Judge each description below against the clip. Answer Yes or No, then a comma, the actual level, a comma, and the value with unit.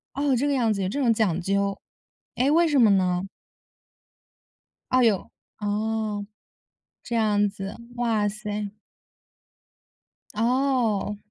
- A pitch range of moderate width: Yes, average, 3.3 semitones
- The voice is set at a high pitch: Yes, high, 215 Hz